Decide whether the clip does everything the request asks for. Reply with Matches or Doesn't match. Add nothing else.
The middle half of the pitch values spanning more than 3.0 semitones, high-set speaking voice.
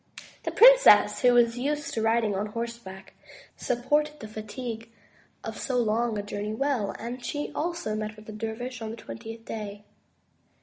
Doesn't match